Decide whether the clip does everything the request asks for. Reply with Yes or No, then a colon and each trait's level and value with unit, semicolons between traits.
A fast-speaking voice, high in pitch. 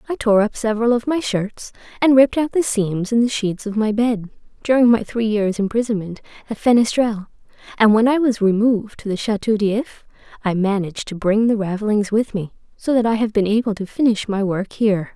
Yes: fast, 210 wpm; high, 220 Hz